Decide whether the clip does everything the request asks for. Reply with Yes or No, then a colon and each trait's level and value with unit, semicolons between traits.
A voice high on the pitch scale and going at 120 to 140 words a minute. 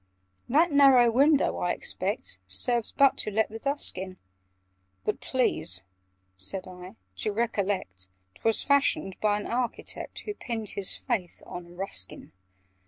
Yes: high, 220 Hz; slow, 135 wpm